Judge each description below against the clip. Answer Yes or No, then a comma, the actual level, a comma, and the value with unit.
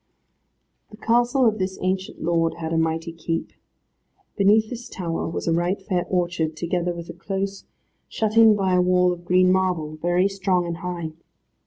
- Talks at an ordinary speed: Yes, average, 175 wpm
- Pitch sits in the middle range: Yes, medium, 180 Hz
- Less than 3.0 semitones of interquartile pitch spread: Yes, narrow, 2.6 semitones